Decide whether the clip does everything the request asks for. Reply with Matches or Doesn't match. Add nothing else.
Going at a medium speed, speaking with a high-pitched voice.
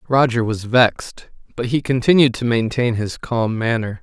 Doesn't match